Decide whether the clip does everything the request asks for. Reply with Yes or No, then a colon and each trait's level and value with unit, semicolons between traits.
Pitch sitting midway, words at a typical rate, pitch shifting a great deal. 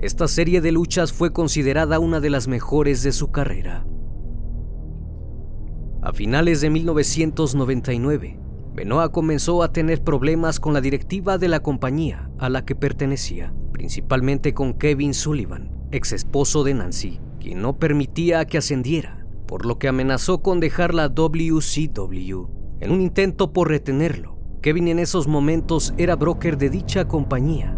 Yes: medium, 145 Hz; average, 145 wpm; wide, 6.3 semitones